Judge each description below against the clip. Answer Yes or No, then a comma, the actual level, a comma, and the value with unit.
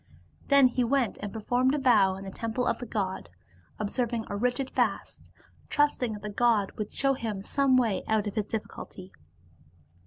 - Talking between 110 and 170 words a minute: No, average, 185 wpm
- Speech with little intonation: No, average, 3.7 semitones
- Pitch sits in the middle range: No, high, 225 Hz